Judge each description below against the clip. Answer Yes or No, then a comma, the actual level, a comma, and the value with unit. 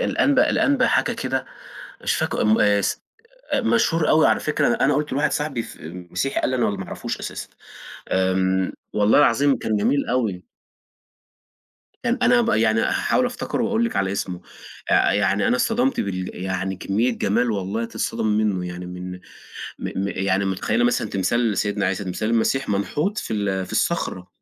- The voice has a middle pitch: No, low, 110 Hz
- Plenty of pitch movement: Yes, wide, 6.2 semitones